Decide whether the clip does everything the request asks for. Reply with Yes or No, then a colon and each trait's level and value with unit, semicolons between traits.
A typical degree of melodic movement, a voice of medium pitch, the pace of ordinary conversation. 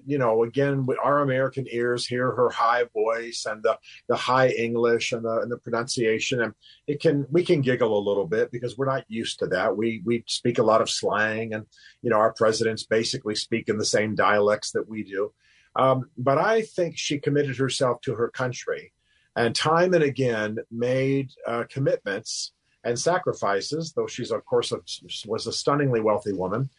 No: average, 4.2 semitones; low, 125 Hz; average, 190 wpm